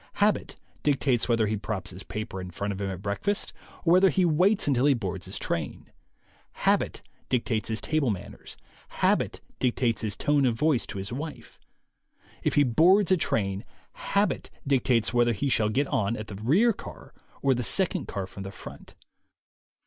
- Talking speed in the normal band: Yes, average, 175 wpm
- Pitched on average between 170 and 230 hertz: No, low, 120 Hz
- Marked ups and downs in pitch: Yes, wide, 6.5 semitones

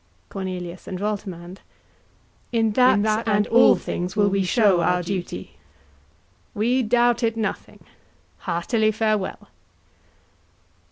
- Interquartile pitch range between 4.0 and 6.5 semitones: No, average, 3.4 semitones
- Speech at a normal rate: No, slow, 110 wpm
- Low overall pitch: No, high, 210 Hz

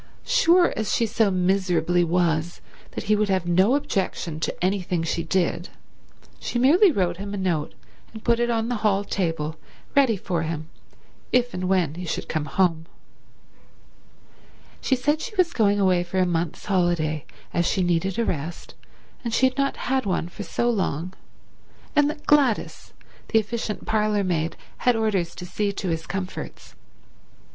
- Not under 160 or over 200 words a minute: Yes, average, 165 wpm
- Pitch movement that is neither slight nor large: Yes, average, 4.8 semitones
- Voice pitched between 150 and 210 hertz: Yes, high, 190 Hz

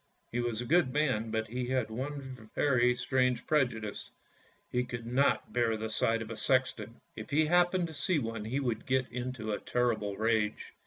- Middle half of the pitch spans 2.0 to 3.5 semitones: Yes, average, 2.9 semitones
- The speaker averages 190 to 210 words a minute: Yes, average, 195 wpm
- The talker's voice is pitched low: Yes, low, 125 Hz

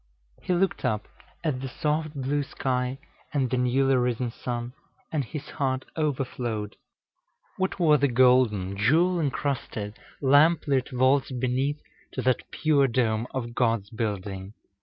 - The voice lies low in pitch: Yes, low, 130 Hz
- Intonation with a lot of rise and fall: No, average, 3.3 semitones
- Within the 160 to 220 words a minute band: No, average, 140 wpm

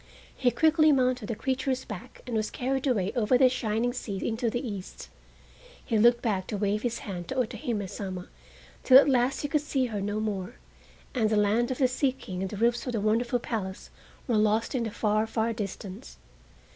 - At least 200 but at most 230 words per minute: Yes, fast, 205 wpm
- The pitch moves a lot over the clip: No, average, 3.3 semitones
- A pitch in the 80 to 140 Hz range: No, high, 230 Hz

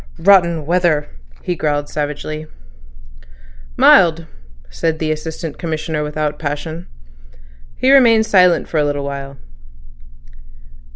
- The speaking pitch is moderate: Yes, medium, 155 Hz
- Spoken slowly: Yes, slow, 105 wpm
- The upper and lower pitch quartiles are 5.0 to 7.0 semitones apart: No, average, 2.7 semitones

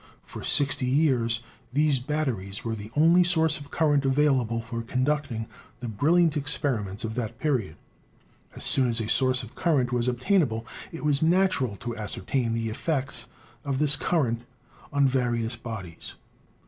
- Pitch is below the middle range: Yes, low, 130 Hz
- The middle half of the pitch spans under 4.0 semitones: No, average, 4.4 semitones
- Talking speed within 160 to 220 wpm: No, average, 150 wpm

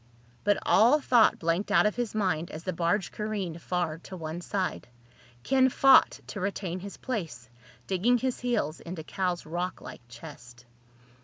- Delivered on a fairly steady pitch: No, average, 4.5 semitones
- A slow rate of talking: No, average, 155 wpm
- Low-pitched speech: No, medium, 185 Hz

